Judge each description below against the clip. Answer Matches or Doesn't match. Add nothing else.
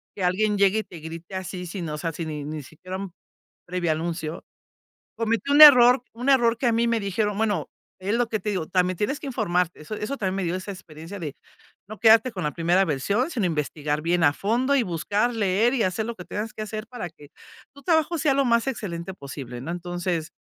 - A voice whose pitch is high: Matches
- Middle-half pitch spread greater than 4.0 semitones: Matches